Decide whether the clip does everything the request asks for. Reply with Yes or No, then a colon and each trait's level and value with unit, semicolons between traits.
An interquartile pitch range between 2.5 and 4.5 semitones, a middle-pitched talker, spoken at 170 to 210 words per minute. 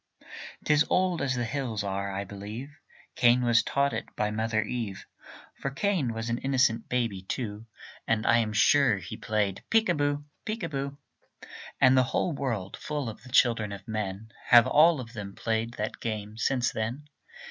No: average, 4.2 semitones; low, 115 Hz; average, 180 wpm